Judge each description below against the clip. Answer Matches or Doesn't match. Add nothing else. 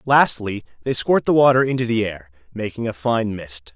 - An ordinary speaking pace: Matches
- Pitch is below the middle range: Matches